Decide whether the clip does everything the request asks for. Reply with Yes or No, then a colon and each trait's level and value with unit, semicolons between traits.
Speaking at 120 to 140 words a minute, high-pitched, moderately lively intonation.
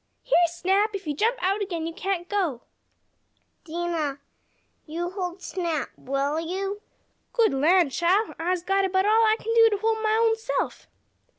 No: average, 165 wpm; very high, 370 Hz; average, 4.0 semitones